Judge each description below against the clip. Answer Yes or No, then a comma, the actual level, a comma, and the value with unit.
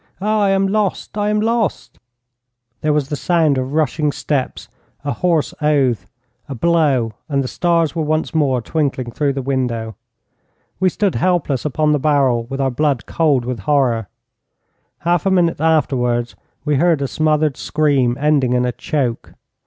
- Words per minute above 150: Yes, average, 165 wpm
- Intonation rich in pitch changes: No, average, 4.0 semitones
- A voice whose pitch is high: No, medium, 150 Hz